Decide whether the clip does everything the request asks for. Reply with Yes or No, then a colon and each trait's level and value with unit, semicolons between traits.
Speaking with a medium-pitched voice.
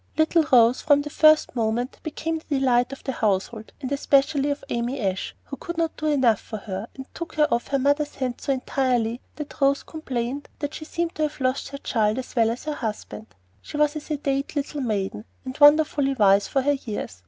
No: very high, 270 Hz